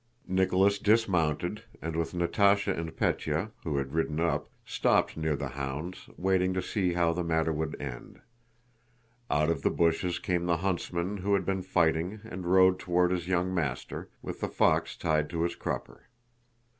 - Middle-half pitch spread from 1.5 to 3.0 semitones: Yes, narrow, 2.5 semitones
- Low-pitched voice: Yes, very low, 85 Hz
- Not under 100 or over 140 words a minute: No, average, 170 wpm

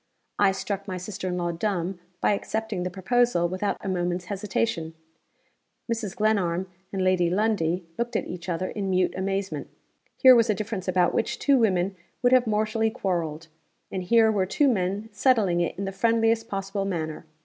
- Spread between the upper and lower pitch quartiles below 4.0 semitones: Yes, average, 3.4 semitones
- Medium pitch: No, high, 195 Hz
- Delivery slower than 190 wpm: Yes, average, 175 wpm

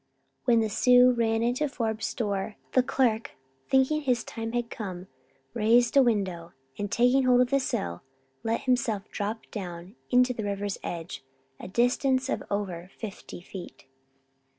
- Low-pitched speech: No, high, 225 Hz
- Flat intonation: No, average, 3.7 semitones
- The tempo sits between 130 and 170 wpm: Yes, average, 150 wpm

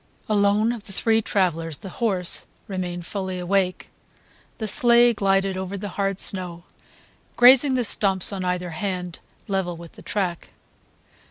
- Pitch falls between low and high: No, high, 195 Hz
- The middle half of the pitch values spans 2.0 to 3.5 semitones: Yes, narrow, 2.6 semitones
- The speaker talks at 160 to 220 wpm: No, average, 145 wpm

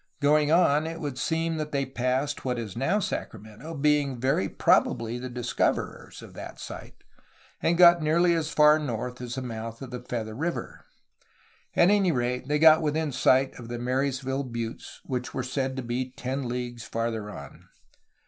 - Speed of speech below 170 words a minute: No, average, 175 wpm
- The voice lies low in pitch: Yes, low, 130 Hz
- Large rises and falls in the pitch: No, average, 3.8 semitones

